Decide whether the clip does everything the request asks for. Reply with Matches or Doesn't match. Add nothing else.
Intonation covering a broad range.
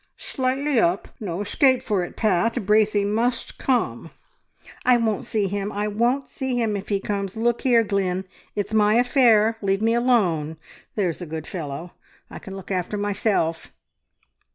Doesn't match